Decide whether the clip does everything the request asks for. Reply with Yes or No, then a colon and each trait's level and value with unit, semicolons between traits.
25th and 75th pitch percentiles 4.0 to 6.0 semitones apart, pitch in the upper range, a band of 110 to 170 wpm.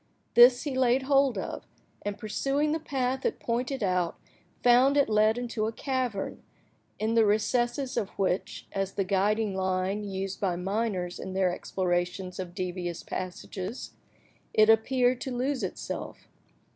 Yes: average, 4.9 semitones; high, 215 Hz; average, 145 wpm